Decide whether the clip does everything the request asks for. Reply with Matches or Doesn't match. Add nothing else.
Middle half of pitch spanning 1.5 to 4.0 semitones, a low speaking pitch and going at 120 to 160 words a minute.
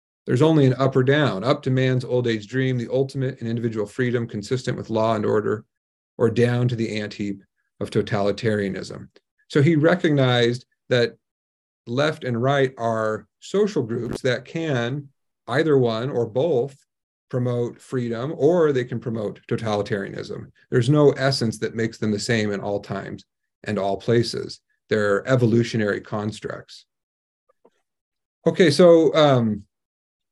Matches